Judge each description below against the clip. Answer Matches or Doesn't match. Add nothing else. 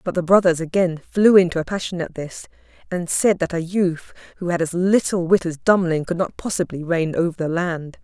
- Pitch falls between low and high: Matches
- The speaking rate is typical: Doesn't match